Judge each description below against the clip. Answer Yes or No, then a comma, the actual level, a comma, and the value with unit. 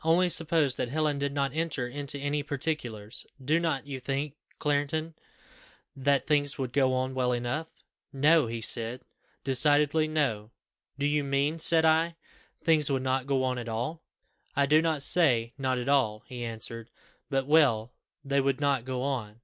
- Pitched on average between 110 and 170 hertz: Yes, medium, 140 Hz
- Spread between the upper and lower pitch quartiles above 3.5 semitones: No, average, 3.0 semitones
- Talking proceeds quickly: No, average, 175 wpm